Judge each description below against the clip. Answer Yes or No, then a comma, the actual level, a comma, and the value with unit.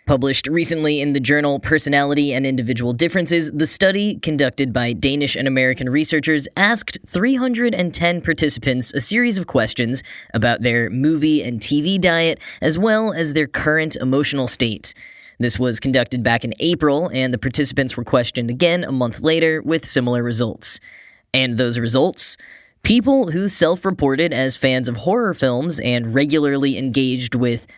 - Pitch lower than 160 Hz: Yes, medium, 140 Hz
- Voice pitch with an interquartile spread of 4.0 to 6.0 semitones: Yes, average, 4.6 semitones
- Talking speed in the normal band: Yes, average, 155 wpm